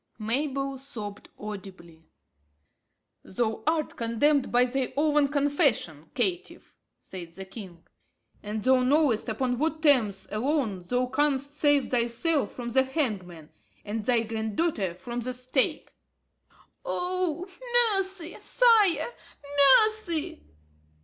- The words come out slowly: Yes, slow, 110 wpm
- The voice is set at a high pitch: Yes, very high, 255 Hz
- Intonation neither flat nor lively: No, wide, 5.8 semitones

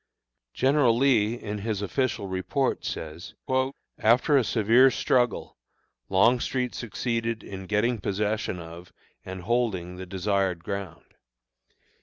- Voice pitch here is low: Yes, low, 105 Hz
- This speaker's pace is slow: Yes, slow, 110 wpm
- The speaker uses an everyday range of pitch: Yes, average, 4.3 semitones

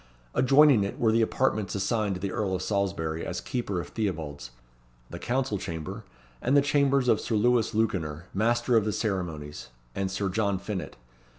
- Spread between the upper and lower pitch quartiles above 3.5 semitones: Yes, average, 4.2 semitones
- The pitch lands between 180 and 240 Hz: No, low, 105 Hz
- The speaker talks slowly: No, average, 175 wpm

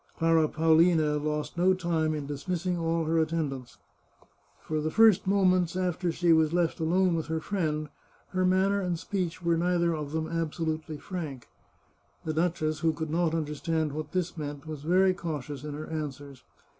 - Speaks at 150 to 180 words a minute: Yes, average, 170 wpm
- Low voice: No, medium, 160 Hz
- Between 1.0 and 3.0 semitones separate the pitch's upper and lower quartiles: Yes, narrow, 2.4 semitones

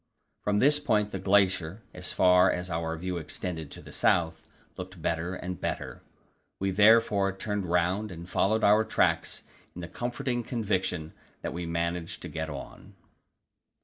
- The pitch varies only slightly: No, average, 3.4 semitones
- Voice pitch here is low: Yes, very low, 90 Hz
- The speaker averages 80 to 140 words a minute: No, average, 160 wpm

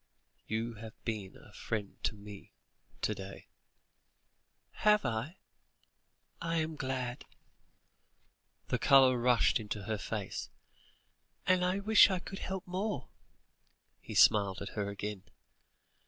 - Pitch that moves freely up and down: Yes, wide, 8.4 semitones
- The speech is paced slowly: Yes, slow, 120 wpm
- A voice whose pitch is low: Yes, low, 120 Hz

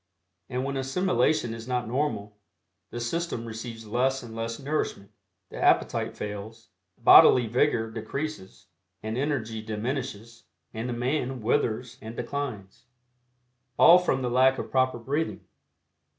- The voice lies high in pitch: No, low, 120 Hz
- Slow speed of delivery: Yes, slow, 130 wpm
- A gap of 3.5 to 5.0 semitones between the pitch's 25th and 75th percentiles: No, average, 3.1 semitones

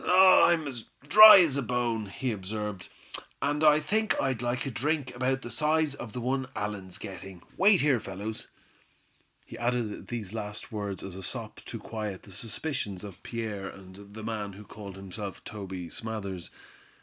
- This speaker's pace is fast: No, average, 170 wpm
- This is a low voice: Yes, low, 110 Hz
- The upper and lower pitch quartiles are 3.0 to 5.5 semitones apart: Yes, average, 5.0 semitones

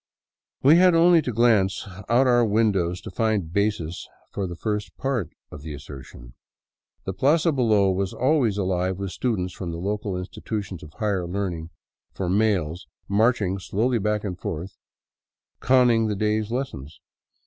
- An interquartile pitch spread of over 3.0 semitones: Yes, average, 4.3 semitones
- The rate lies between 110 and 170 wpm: Yes, average, 150 wpm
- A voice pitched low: Yes, low, 100 Hz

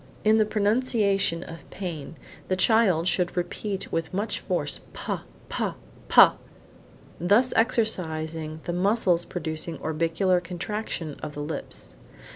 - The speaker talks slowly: Yes, slow, 120 wpm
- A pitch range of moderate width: Yes, average, 4.3 semitones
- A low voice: No, medium, 180 Hz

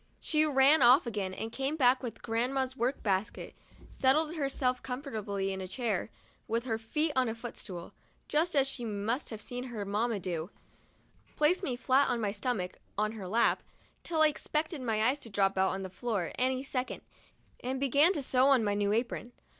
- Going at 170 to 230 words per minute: Yes, average, 190 wpm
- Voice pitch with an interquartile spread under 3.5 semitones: No, average, 4.4 semitones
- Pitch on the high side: Yes, high, 245 Hz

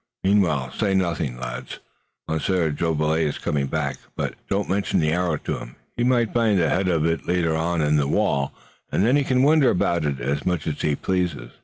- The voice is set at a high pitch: No, very low, 80 Hz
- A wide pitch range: No, average, 4.5 semitones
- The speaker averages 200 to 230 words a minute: Yes, fast, 205 wpm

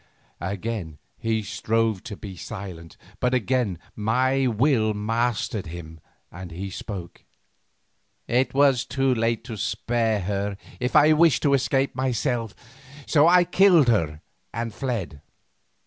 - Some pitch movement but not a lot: Yes, average, 4.7 semitones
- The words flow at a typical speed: No, slow, 130 wpm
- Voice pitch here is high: No, low, 115 Hz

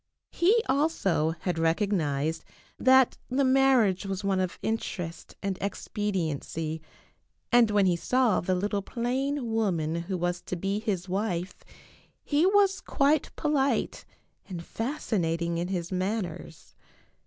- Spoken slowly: Yes, slow, 130 wpm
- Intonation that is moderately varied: No, wide, 6.6 semitones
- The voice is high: Yes, high, 195 Hz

